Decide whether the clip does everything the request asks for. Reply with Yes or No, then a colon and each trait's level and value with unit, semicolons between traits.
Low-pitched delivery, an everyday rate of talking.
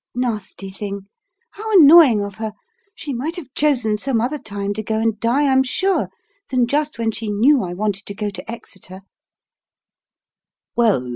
No: high, 225 Hz; average, 160 wpm